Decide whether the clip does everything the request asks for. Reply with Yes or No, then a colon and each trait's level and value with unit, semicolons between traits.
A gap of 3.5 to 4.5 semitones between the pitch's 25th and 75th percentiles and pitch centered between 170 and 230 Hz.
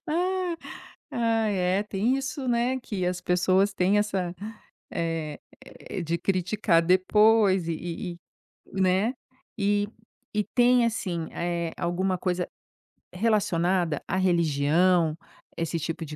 Yes: average, 3.8 semitones; medium, 185 Hz